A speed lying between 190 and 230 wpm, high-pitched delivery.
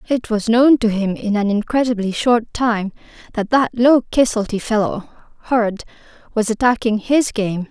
No: average, 155 wpm; high, 225 Hz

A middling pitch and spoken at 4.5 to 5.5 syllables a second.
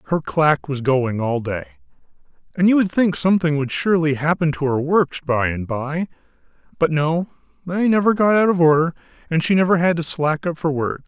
Yes: medium, 160 Hz; 5.3 syllables/s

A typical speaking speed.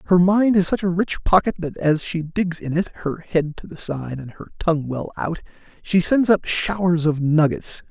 No: fast, 220 wpm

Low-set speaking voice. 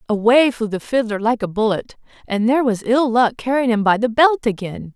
No: high, 230 Hz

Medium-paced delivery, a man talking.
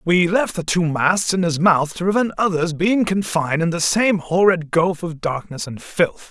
No: fast, 210 wpm; male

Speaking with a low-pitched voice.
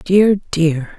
No: medium, 175 Hz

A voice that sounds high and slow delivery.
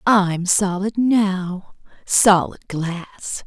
Yes: high, 195 Hz; slow, 85 wpm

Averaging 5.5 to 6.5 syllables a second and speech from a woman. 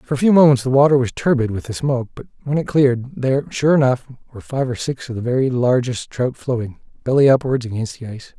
No: 6.4 syllables/s; male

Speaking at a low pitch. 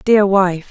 No: high, 195 Hz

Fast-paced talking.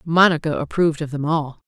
No: average, 180 wpm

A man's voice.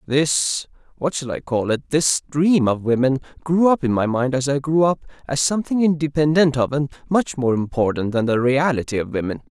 Yes: male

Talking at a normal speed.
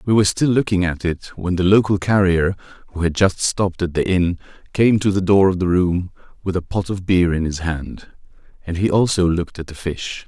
No: fast, 230 wpm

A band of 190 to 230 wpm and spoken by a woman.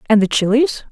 Yes: average, 200 wpm; female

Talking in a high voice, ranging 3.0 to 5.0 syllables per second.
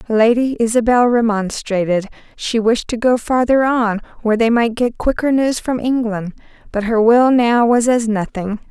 Yes: high, 230 Hz; 4.6 syllables/s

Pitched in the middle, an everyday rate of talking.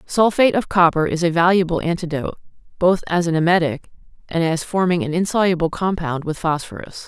Yes: medium, 170 Hz; average, 160 wpm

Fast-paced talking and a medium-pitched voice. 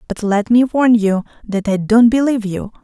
No: fast, 210 wpm; high, 220 Hz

